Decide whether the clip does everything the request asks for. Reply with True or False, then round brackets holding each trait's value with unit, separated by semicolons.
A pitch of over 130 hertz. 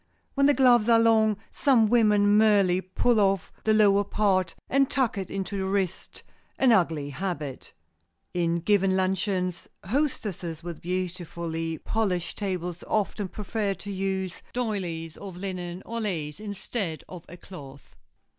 True (190 Hz)